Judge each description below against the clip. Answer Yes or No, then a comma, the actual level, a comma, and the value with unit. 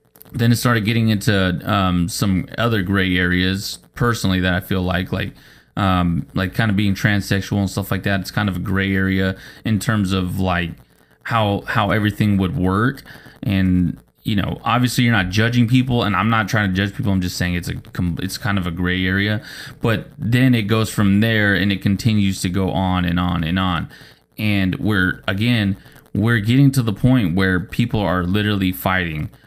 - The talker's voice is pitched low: Yes, low, 100 Hz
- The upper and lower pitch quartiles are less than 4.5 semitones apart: Yes, average, 3.2 semitones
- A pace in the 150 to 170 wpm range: No, average, 195 wpm